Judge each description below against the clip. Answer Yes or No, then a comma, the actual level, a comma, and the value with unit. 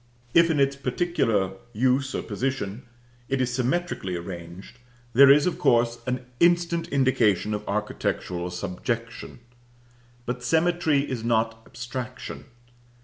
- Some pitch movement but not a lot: Yes, average, 4.5 semitones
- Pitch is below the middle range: Yes, low, 125 Hz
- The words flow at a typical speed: No, slow, 120 wpm